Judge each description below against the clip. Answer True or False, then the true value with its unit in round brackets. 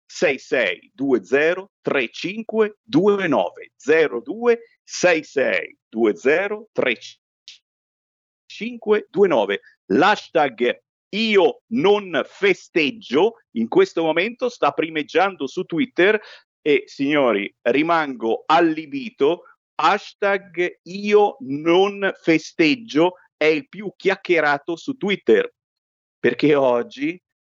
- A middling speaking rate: False (70 wpm)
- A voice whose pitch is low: False (210 Hz)